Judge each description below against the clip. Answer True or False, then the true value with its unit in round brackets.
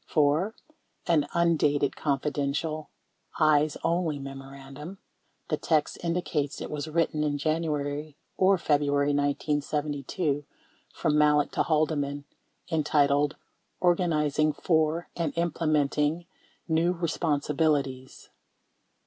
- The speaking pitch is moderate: True (150 Hz)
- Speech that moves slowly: True (100 wpm)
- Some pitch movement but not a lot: False (2.1 semitones)